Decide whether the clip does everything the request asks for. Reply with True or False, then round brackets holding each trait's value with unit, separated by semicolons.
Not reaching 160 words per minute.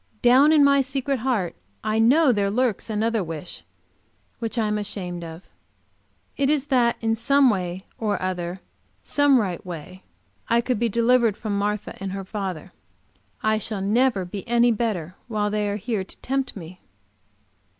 False (165 wpm)